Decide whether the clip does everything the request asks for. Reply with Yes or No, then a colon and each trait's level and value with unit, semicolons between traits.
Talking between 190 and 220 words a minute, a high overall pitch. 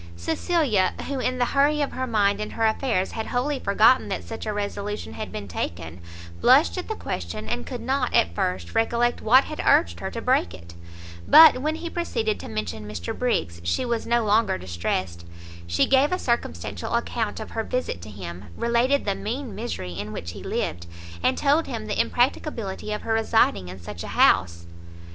Yes: average, 195 wpm; high, 215 Hz